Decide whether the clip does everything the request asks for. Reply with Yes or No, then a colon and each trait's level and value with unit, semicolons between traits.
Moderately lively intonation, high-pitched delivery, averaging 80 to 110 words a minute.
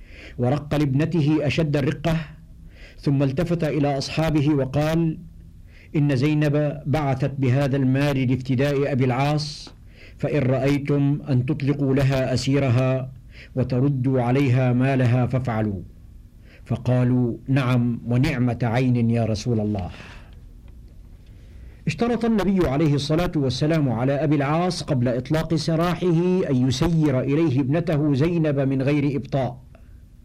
No: average, 3.7 semitones; low, 135 Hz; average, 105 wpm